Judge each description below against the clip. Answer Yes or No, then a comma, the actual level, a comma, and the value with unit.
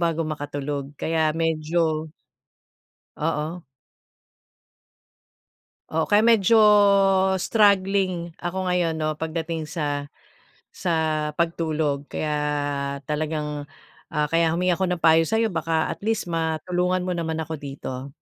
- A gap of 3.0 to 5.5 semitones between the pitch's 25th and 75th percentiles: No, narrow, 2.4 semitones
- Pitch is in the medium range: Yes, medium, 160 Hz